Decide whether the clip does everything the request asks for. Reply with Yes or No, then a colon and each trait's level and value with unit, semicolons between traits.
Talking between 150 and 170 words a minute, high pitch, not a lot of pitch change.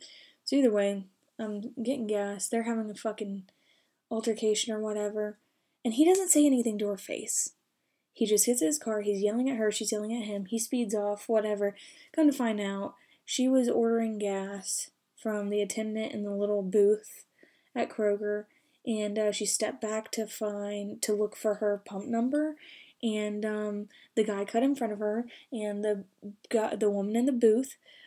No: average, 180 wpm; high, 215 Hz; narrow, 2.3 semitones